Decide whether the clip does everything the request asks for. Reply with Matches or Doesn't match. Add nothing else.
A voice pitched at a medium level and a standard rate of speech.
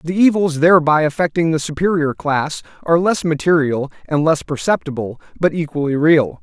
Matches